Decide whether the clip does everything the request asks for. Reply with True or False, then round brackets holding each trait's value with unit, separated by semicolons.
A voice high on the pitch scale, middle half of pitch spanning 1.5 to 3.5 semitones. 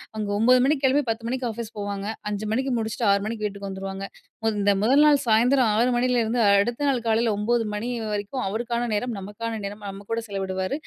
True (225 Hz; 3.0 semitones)